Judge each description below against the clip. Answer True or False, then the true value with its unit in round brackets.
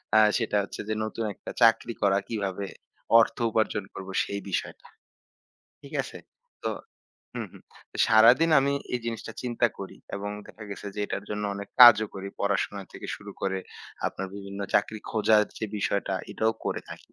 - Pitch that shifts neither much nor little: False (2.1 semitones)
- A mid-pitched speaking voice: False (105 Hz)